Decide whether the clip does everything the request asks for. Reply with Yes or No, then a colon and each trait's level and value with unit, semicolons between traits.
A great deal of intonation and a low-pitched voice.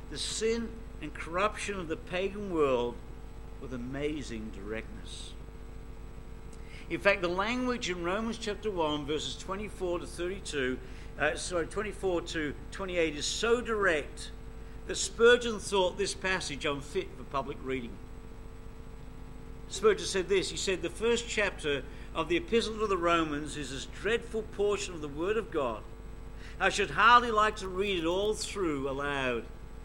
No: wide, 6.4 semitones; medium, 175 Hz